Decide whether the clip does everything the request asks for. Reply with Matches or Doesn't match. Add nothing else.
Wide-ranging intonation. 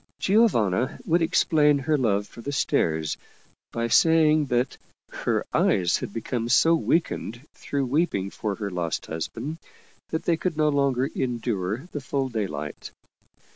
Matches